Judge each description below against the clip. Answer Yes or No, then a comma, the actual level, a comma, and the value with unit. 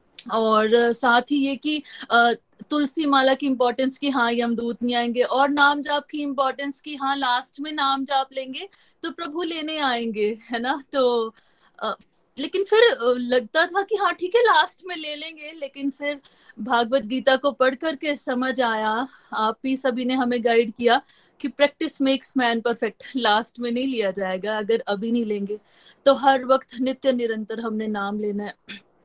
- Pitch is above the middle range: Yes, very high, 260 Hz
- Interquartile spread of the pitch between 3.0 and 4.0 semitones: Yes, average, 3.3 semitones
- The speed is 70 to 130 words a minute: No, average, 180 wpm